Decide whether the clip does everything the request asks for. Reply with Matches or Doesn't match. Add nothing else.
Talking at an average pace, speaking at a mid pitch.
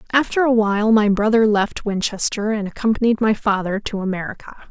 Doesn't match